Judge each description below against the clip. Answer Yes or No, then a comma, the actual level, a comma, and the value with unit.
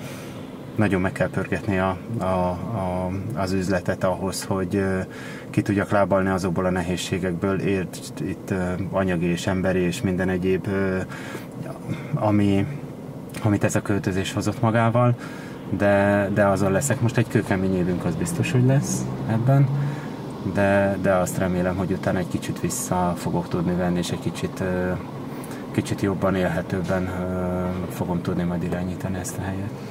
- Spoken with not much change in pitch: Yes, narrow, 2.0 semitones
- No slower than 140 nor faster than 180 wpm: Yes, average, 150 wpm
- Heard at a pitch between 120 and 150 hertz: No, very low, 95 Hz